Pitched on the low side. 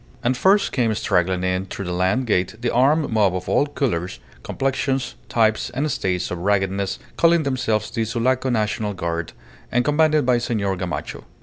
Yes: low, 110 Hz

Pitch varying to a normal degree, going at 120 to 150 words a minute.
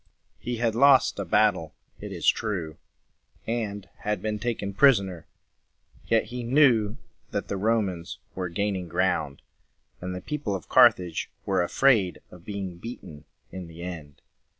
Yes: average, 4.2 semitones; average, 145 wpm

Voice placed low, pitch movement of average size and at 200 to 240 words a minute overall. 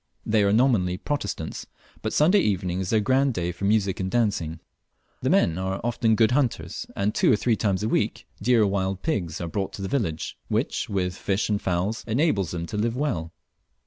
Yes: low, 100 Hz; average, 4.2 semitones; fast, 205 wpm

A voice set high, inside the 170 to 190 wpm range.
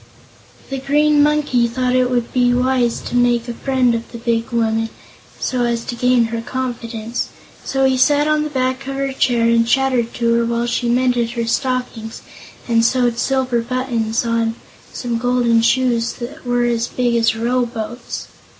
Yes: high, 240 Hz; average, 175 wpm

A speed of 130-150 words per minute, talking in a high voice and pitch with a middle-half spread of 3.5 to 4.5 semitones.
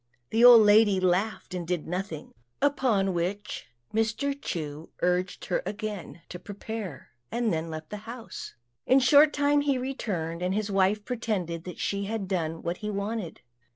No: average, 165 wpm; high, 200 Hz; average, 4.1 semitones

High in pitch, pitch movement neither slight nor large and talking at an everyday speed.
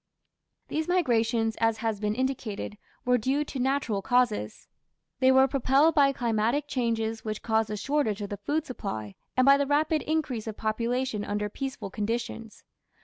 Yes: high, 235 Hz; average, 4.0 semitones; average, 160 wpm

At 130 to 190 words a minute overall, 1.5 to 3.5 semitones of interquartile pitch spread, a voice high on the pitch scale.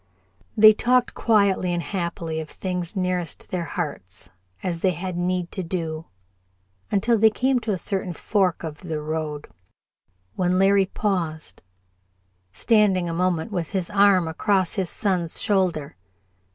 No: average, 140 wpm; average, 3.2 semitones; medium, 180 Hz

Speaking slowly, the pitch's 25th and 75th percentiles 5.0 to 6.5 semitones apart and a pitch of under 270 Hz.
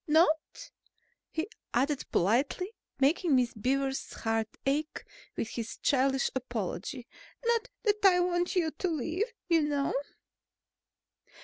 No: slow, 115 wpm; wide, 5.4 semitones; very high, 290 Hz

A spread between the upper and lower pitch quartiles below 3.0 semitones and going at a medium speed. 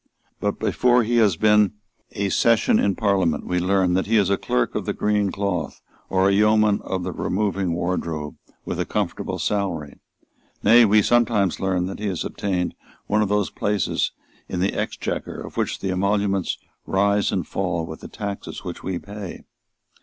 Yes: narrow, 2.4 semitones; average, 175 wpm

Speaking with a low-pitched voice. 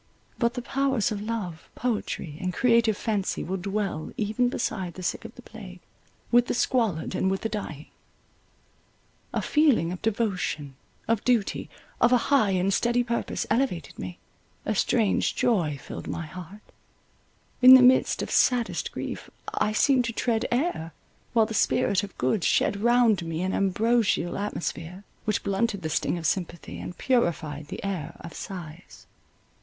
No: high, 205 Hz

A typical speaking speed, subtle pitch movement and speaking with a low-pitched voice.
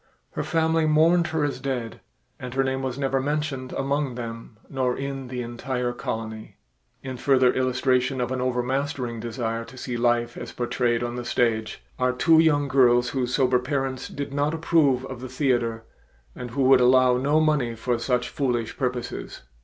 Yes: average, 170 wpm; narrow, 2.2 semitones; low, 130 Hz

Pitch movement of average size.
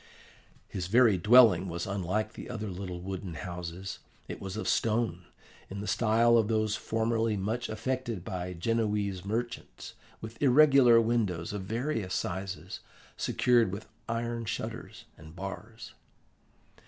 Yes: average, 3.8 semitones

